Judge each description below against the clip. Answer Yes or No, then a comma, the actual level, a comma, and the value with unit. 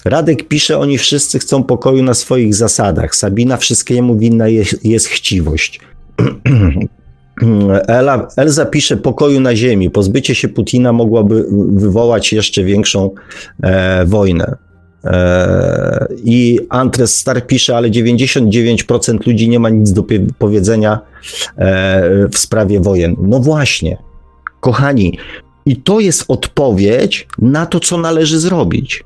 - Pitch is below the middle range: Yes, low, 115 Hz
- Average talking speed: Yes, average, 120 wpm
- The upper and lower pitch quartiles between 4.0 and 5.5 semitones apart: Yes, average, 4.4 semitones